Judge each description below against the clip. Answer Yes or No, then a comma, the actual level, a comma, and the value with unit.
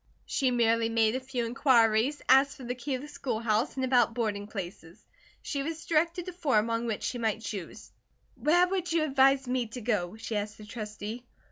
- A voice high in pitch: Yes, high, 240 Hz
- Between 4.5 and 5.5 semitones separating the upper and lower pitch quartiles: No, average, 3.9 semitones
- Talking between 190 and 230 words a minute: Yes, average, 200 wpm